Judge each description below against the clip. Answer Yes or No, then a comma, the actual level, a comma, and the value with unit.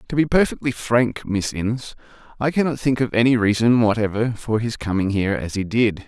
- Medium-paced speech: No, fast, 210 wpm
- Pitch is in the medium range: No, low, 115 Hz